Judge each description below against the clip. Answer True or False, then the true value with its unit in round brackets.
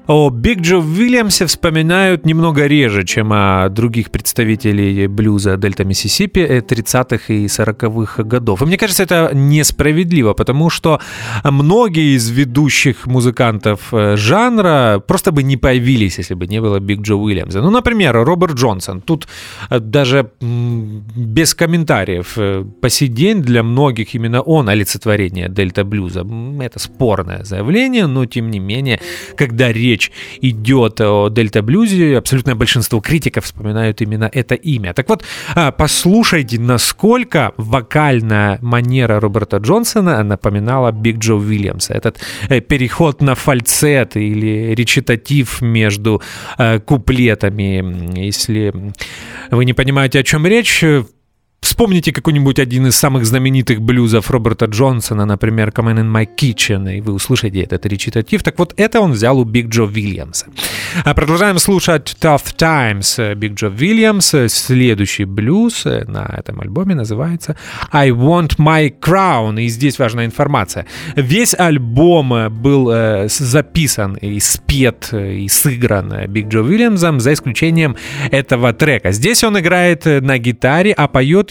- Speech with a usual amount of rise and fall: False (5.9 semitones)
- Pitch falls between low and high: False (125 Hz)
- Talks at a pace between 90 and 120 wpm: False (130 wpm)